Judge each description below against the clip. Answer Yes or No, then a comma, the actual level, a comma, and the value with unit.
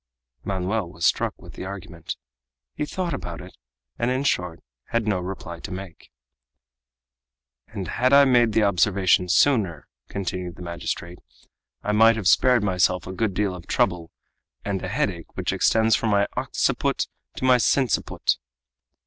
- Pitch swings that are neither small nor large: Yes, average, 4.0 semitones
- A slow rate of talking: No, average, 155 wpm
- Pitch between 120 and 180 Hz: No, very low, 95 Hz